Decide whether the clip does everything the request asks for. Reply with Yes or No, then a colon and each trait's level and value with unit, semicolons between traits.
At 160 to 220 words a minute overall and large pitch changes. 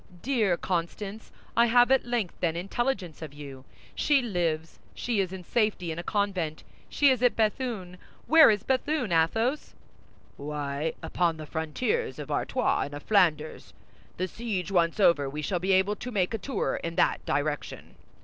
Yes: average, 170 wpm; wide, 6.5 semitones